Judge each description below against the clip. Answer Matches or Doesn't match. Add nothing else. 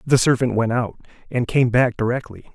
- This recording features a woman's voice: Doesn't match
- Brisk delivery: Doesn't match